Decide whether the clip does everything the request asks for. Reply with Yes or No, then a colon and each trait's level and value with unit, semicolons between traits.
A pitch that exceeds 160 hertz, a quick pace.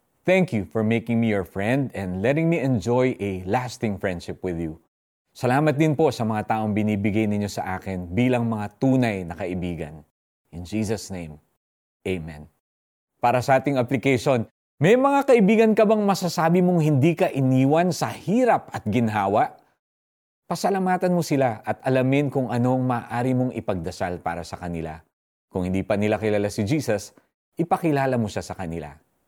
No: low, 115 Hz; fast, 160 wpm